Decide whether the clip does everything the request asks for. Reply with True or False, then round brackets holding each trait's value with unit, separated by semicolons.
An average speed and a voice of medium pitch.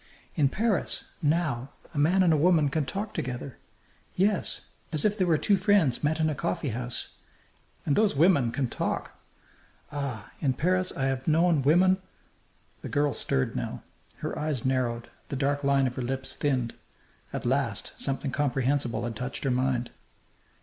True (165 wpm; 145 Hz)